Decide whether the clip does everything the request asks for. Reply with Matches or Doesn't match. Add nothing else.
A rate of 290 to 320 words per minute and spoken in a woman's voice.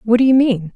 Matches